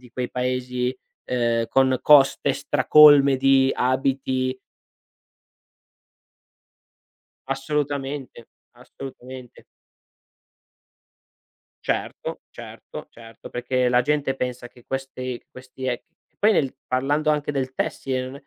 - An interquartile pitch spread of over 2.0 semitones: No, narrow, 1.5 semitones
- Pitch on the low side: Yes, low, 130 Hz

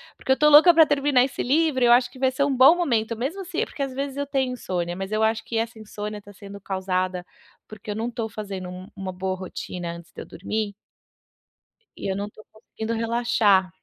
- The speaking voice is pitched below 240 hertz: Yes, high, 220 Hz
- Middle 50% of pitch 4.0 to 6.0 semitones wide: Yes, average, 5.3 semitones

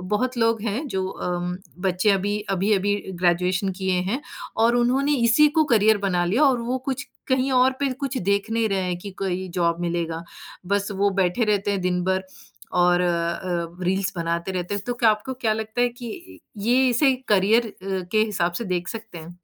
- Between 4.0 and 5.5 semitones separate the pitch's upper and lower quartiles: Yes, average, 4.5 semitones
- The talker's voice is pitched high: Yes, high, 200 Hz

